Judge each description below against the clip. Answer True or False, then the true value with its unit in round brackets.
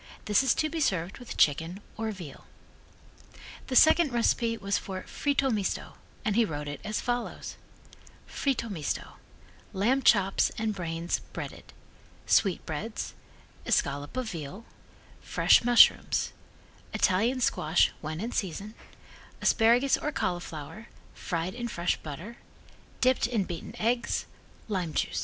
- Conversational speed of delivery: False (125 wpm)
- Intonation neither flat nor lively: False (5.8 semitones)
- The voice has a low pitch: False (210 Hz)